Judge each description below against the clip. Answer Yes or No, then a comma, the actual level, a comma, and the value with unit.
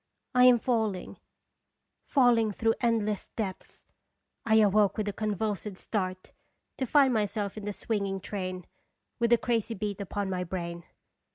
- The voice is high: Yes, high, 210 Hz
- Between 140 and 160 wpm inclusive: Yes, average, 150 wpm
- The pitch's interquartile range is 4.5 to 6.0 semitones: No, average, 2.8 semitones